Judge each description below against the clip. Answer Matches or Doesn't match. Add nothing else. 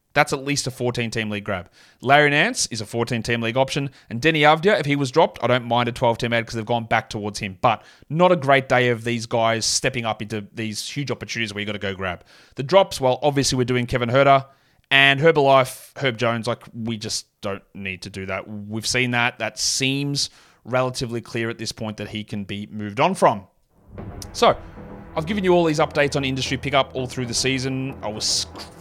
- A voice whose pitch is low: Matches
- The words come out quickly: Matches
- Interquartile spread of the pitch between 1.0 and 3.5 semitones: Doesn't match